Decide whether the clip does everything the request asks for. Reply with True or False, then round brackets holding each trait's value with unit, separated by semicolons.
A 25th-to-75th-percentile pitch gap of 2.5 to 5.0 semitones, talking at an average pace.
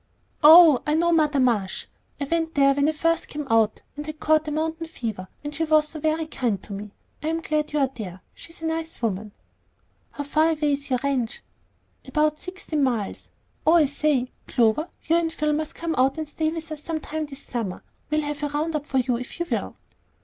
False (3.2 semitones; 215 wpm)